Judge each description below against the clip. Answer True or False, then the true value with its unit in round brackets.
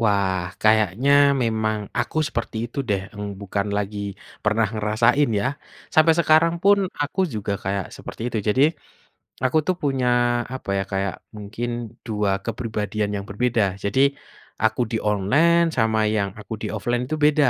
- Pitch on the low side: True (110 Hz)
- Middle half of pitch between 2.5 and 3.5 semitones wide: False (4.0 semitones)